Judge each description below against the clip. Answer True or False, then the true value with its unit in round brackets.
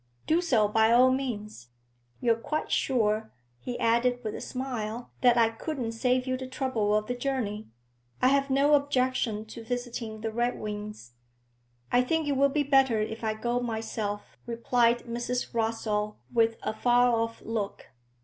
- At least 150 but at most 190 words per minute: True (160 wpm)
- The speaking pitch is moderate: False (235 Hz)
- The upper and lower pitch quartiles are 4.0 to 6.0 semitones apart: False (2.8 semitones)